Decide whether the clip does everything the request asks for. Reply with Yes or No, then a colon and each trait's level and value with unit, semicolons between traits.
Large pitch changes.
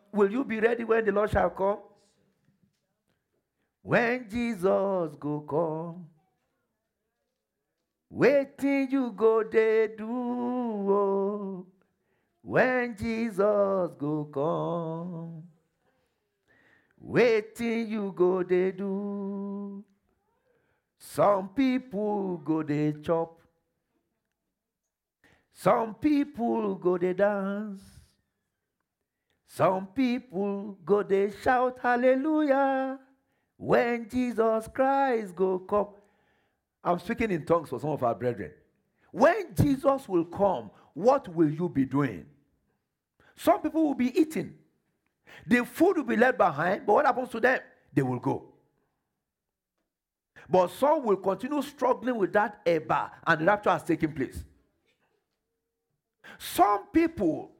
Yes: wide, 5.9 semitones